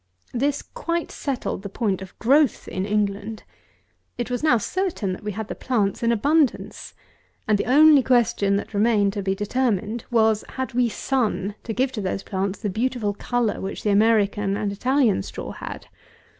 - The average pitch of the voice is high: Yes, high, 220 Hz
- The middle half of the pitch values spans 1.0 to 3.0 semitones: No, average, 4.0 semitones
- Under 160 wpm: No, average, 180 wpm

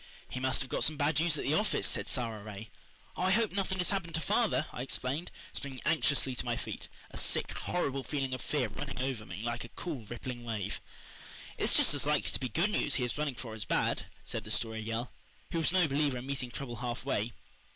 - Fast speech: Yes, fast, 235 wpm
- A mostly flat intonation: No, average, 4.6 semitones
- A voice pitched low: Yes, low, 130 Hz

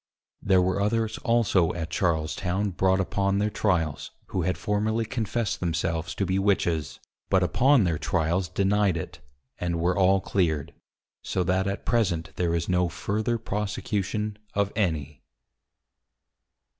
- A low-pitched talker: Yes, very low, 95 Hz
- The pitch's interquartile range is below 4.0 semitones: Yes, average, 3.5 semitones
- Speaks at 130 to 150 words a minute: Yes, average, 145 wpm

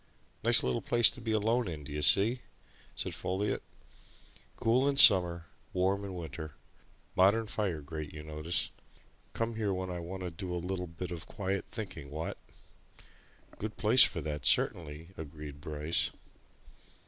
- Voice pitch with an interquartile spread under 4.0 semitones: No, average, 4.8 semitones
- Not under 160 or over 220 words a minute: No, average, 150 wpm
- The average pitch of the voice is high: No, very low, 90 Hz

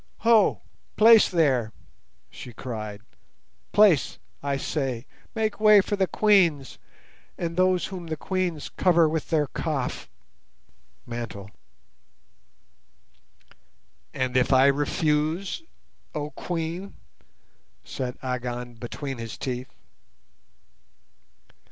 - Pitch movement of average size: No, wide, 6.4 semitones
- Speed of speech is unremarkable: No, slow, 95 wpm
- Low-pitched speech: No, medium, 150 Hz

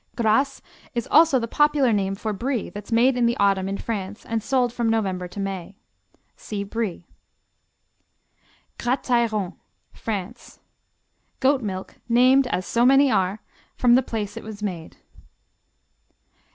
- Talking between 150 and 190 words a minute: No, average, 140 wpm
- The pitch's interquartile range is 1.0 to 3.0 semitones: No, average, 3.9 semitones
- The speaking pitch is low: No, high, 225 Hz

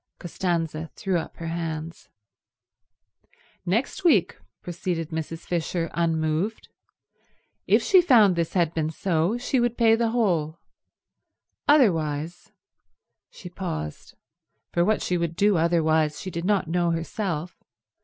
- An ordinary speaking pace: No, slow, 120 wpm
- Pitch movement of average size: Yes, average, 3.7 semitones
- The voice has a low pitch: No, medium, 170 Hz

